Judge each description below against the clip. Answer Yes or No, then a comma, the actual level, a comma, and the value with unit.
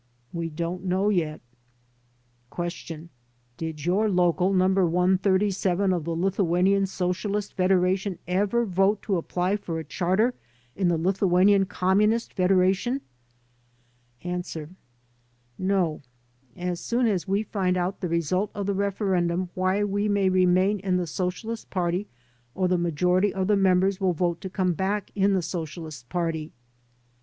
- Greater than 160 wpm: No, average, 140 wpm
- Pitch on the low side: No, medium, 185 Hz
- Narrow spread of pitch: Yes, narrow, 2.0 semitones